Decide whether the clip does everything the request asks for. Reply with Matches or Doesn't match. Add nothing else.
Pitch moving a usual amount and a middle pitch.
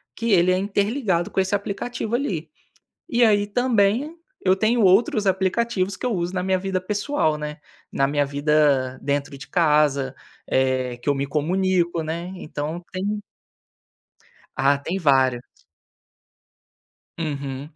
Doesn't match